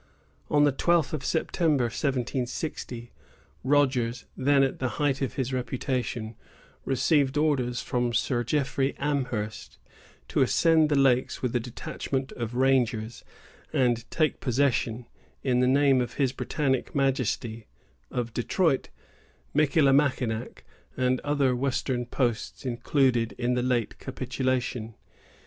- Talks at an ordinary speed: No, slow, 120 wpm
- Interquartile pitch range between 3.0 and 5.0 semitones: No, narrow, 2.4 semitones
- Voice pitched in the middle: No, low, 130 Hz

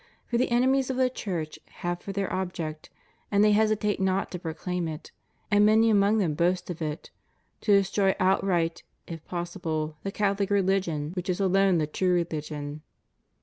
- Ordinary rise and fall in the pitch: Yes, average, 3.4 semitones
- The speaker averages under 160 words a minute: No, average, 180 wpm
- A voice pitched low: No, medium, 185 Hz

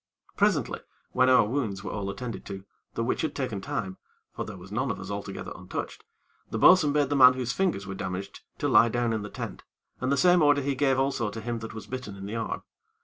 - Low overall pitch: Yes, low, 115 Hz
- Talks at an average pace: No, fast, 235 wpm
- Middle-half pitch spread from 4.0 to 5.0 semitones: Yes, average, 4.7 semitones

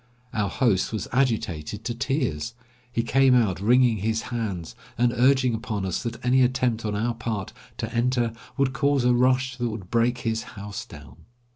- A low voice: Yes, low, 115 Hz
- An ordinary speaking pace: Yes, average, 175 wpm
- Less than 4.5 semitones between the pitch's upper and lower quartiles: Yes, average, 2.9 semitones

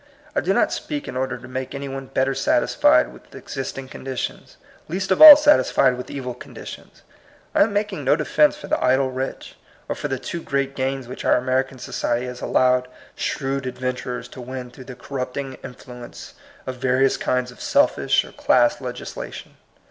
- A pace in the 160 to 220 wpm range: Yes, average, 180 wpm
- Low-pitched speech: Yes, low, 130 Hz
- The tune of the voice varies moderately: No, narrow, 1.4 semitones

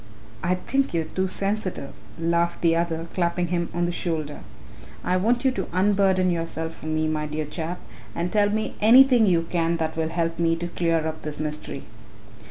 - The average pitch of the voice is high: No, medium, 170 Hz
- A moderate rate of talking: Yes, average, 190 wpm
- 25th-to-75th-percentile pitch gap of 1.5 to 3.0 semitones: Yes, narrow, 2.4 semitones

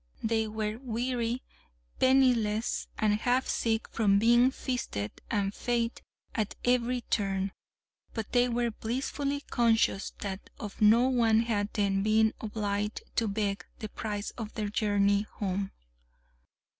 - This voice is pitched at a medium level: No, high, 220 Hz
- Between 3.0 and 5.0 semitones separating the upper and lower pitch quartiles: No, narrow, 2.6 semitones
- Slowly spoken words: Yes, slow, 130 wpm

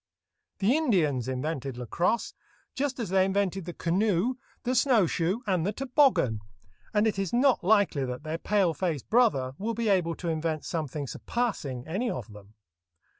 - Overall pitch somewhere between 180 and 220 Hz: Yes, medium, 185 Hz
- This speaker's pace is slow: No, average, 165 wpm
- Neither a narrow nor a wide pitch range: No, wide, 6.7 semitones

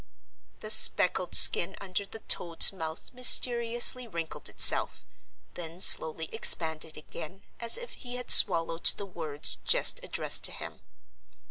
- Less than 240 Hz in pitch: Yes, high, 190 Hz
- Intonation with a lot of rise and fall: Yes, wide, 6.3 semitones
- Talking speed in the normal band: No, slow, 130 wpm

